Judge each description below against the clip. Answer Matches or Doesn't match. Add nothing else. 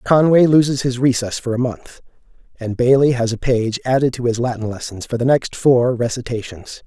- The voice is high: Doesn't match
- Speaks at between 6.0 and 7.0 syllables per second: Doesn't match